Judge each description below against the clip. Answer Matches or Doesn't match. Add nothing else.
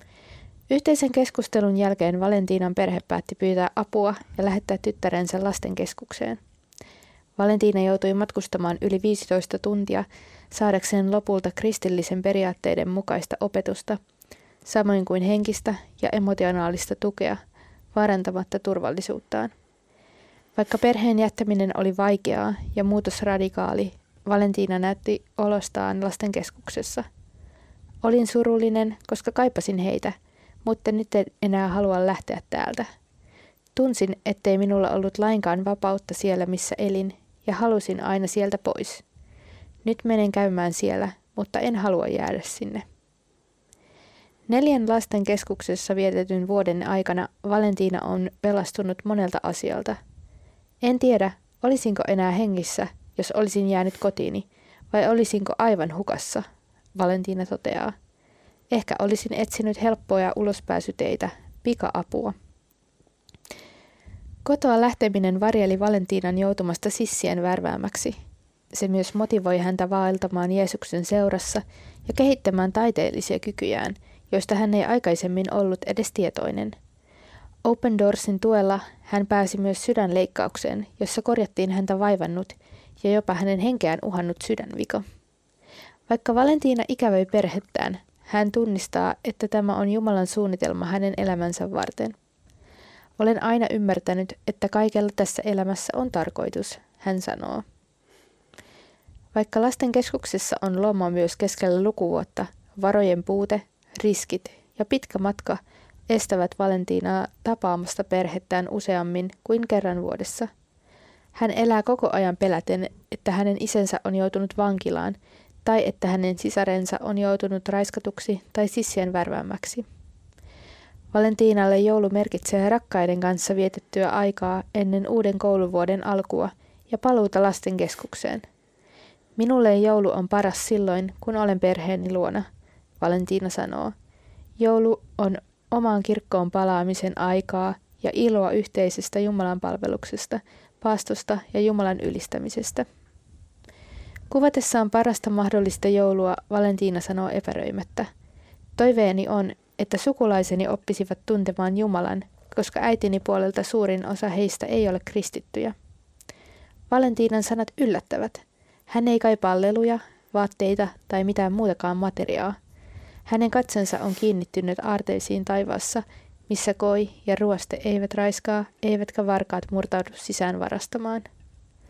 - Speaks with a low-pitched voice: Doesn't match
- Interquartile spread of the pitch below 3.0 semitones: Matches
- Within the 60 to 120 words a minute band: Matches